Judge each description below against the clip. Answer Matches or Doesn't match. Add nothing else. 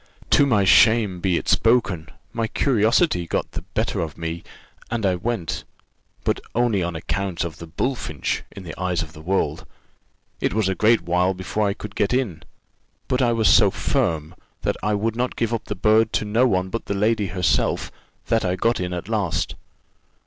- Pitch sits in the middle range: Doesn't match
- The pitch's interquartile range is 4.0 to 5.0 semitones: Matches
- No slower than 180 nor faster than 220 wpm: Matches